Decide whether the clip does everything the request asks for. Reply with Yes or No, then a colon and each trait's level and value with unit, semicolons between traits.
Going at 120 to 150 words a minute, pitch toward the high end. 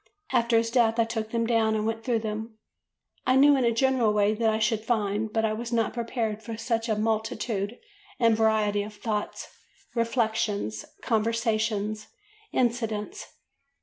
No: average, 160 wpm; high, 225 Hz